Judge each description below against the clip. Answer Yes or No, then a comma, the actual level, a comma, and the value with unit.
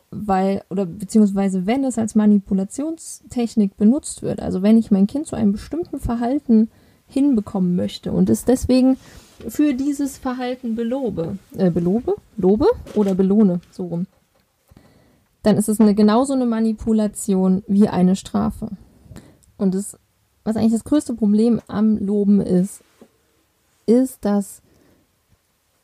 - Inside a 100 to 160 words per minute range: Yes, average, 130 wpm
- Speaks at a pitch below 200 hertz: No, high, 215 Hz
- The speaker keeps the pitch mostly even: No, average, 3.5 semitones